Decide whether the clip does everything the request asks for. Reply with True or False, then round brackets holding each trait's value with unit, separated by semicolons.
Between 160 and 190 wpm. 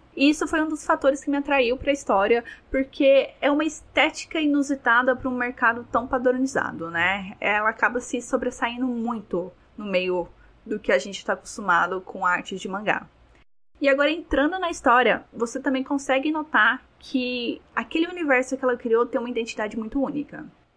True (170 wpm)